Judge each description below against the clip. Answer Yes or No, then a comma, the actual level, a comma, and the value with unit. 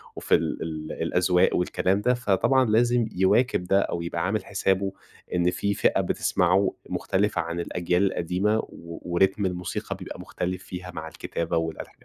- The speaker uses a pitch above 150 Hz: No, very low, 90 Hz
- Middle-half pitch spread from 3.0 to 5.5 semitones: No, narrow, 2.5 semitones